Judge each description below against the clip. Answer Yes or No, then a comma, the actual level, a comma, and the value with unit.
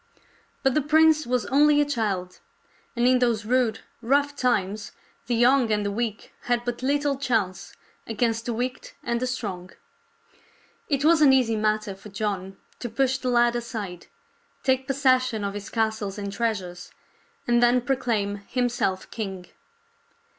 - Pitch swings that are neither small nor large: Yes, average, 3.6 semitones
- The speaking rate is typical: Yes, average, 155 wpm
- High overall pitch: Yes, high, 235 Hz